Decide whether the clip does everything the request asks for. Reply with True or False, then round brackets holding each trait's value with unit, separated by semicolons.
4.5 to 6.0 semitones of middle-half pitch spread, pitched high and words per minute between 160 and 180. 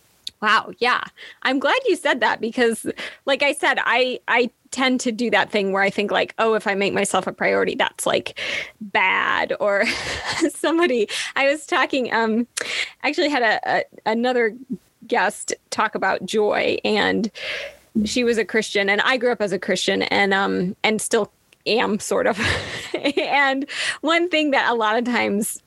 True (4.9 semitones; 235 Hz; 175 wpm)